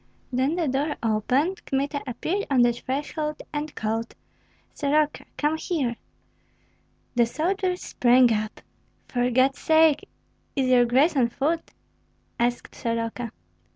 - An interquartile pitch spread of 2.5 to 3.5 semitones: No, average, 4.2 semitones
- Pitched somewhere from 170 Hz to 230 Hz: No, very high, 270 Hz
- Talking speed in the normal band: No, slow, 120 wpm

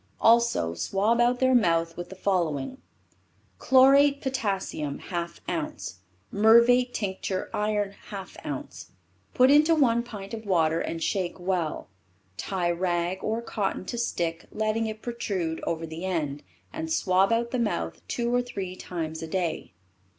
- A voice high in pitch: Yes, high, 195 Hz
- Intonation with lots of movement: Yes, wide, 5.7 semitones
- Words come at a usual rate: Yes, average, 145 wpm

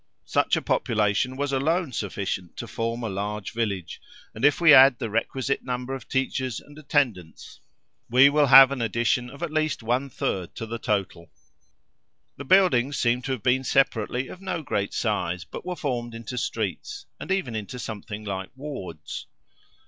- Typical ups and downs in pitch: Yes, average, 4.4 semitones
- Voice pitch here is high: No, low, 125 Hz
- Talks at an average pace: Yes, average, 170 wpm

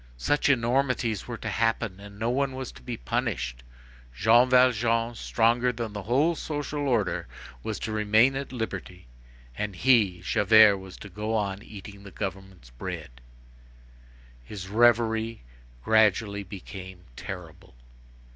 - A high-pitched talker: No, low, 110 Hz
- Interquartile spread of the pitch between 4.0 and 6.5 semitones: No, average, 3.5 semitones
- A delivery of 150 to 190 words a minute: No, slow, 135 wpm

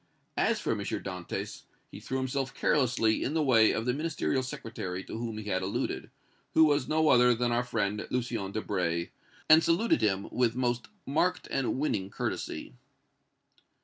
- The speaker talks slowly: No, average, 165 wpm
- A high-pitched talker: No, low, 120 Hz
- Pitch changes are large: No, average, 4.5 semitones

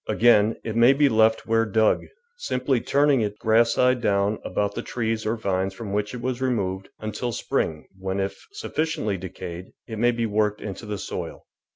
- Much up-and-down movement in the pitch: No, average, 3.1 semitones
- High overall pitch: No, low, 110 Hz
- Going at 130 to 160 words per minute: No, average, 185 wpm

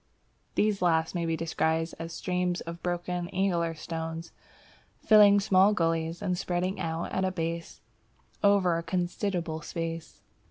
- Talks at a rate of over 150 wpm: No, slow, 135 wpm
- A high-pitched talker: No, medium, 175 Hz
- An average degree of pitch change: No, narrow, 2.1 semitones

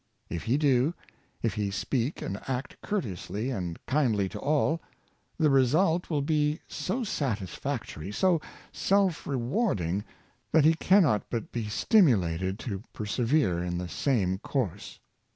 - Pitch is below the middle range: Yes, low, 125 Hz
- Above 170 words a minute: No, average, 145 wpm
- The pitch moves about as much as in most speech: No, wide, 7.7 semitones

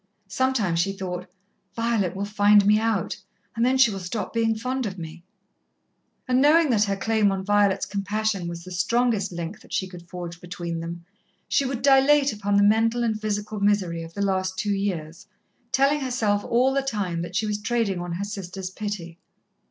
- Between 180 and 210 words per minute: Yes, average, 190 wpm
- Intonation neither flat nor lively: Yes, average, 3.9 semitones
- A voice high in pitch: Yes, high, 205 Hz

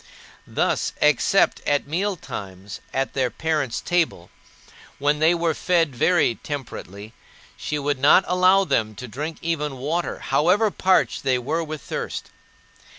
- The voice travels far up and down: No, average, 5.0 semitones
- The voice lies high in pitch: No, medium, 150 Hz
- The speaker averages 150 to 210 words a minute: No, slow, 135 wpm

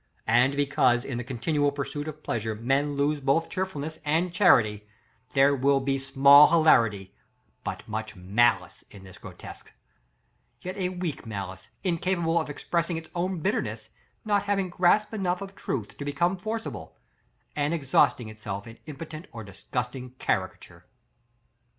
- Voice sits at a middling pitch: Yes, medium, 145 Hz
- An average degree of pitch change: No, wide, 6.1 semitones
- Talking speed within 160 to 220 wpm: No, average, 145 wpm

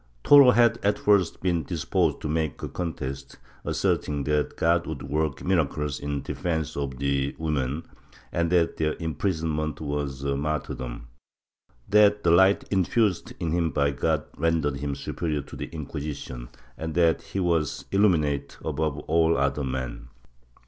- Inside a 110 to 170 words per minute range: Yes, average, 150 wpm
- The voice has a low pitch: Yes, very low, 75 Hz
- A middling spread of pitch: Yes, average, 3.2 semitones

